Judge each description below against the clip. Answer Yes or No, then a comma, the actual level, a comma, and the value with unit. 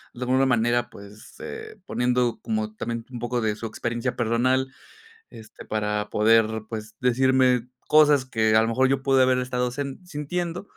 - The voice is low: Yes, low, 125 Hz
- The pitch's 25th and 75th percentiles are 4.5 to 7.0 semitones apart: No, average, 2.7 semitones